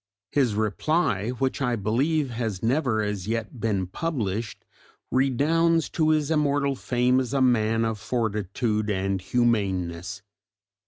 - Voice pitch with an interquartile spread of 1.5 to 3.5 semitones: No, average, 4.7 semitones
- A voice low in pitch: Yes, low, 115 Hz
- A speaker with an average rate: No, slow, 125 wpm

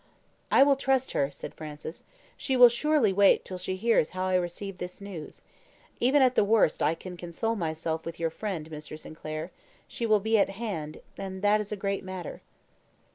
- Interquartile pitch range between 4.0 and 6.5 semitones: Yes, average, 5.1 semitones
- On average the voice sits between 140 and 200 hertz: Yes, high, 190 Hz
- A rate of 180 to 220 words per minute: Yes, average, 190 wpm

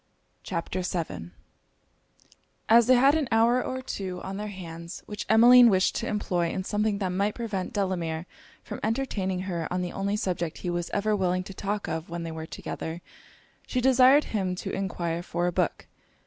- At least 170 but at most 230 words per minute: Yes, average, 180 wpm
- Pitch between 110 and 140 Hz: No, high, 190 Hz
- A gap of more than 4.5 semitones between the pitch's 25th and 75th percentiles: No, average, 3.9 semitones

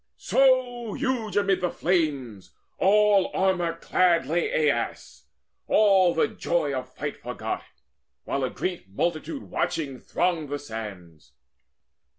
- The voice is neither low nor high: Yes, medium, 170 Hz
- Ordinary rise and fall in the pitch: No, wide, 6.3 semitones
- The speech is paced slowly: Yes, slow, 120 wpm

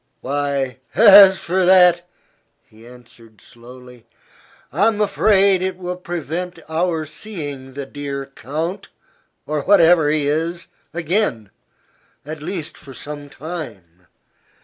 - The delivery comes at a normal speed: No, slow, 110 wpm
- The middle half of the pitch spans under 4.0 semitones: No, average, 4.8 semitones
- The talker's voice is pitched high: No, medium, 155 Hz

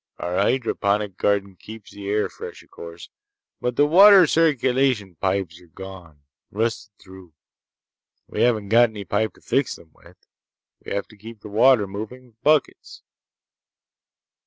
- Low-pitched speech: Yes, low, 105 Hz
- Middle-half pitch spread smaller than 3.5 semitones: No, average, 4.1 semitones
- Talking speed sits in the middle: Yes, average, 145 wpm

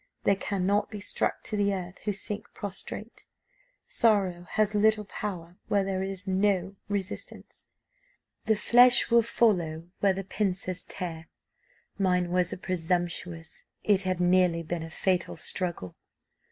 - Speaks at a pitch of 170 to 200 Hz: Yes, high, 190 Hz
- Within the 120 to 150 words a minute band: Yes, average, 140 wpm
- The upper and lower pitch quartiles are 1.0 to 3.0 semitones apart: Yes, narrow, 2.5 semitones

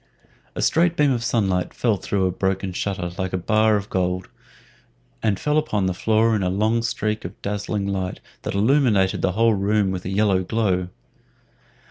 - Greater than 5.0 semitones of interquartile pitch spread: No, average, 3.0 semitones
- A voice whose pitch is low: Yes, low, 100 Hz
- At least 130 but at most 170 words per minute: No, average, 180 wpm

